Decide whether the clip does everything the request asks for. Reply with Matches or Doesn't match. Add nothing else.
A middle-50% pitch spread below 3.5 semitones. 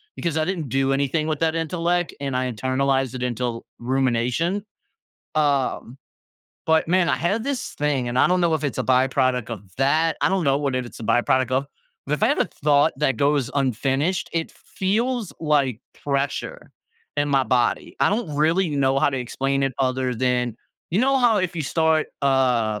Doesn't match